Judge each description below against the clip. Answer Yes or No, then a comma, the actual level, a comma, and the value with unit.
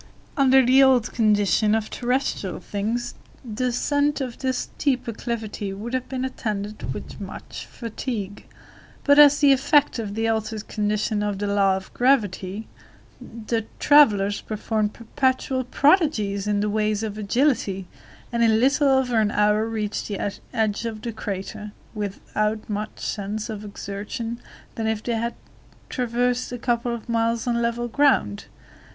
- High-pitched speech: Yes, high, 225 Hz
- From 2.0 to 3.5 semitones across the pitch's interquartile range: Yes, average, 3.1 semitones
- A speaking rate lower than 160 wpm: Yes, average, 150 wpm